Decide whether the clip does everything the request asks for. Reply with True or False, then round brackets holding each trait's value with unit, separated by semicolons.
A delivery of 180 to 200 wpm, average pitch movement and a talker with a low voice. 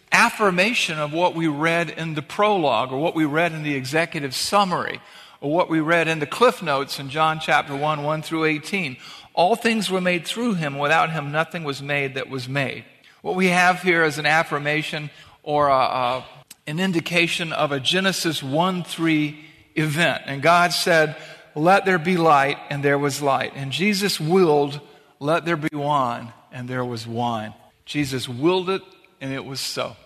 False (185 wpm; 3.4 semitones; 155 Hz)